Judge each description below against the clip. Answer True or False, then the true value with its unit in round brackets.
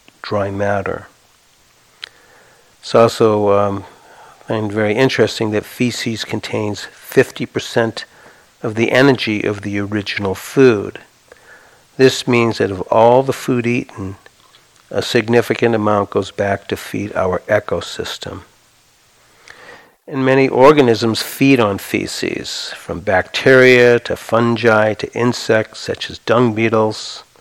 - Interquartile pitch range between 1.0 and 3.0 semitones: True (2.6 semitones)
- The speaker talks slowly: True (115 wpm)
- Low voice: True (115 Hz)